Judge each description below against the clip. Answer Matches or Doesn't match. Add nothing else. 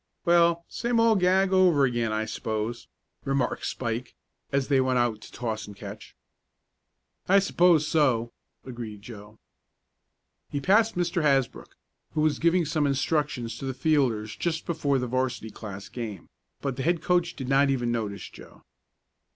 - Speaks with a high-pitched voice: Doesn't match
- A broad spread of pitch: Matches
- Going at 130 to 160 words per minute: Matches